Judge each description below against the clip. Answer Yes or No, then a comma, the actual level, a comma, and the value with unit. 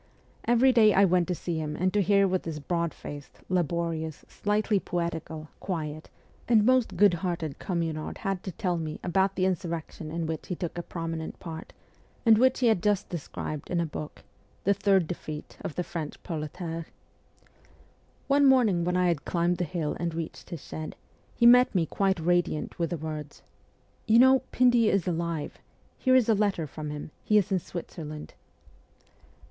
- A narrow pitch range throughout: No, average, 3.7 semitones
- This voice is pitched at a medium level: Yes, medium, 175 Hz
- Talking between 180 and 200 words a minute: Yes, average, 185 wpm